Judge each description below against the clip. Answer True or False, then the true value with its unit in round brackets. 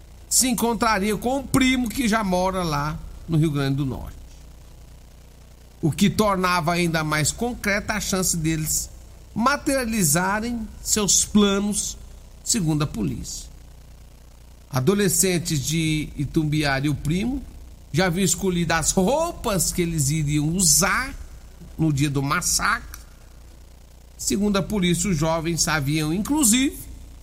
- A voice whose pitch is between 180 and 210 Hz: False (165 Hz)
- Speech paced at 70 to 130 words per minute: True (120 wpm)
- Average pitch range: False (7.0 semitones)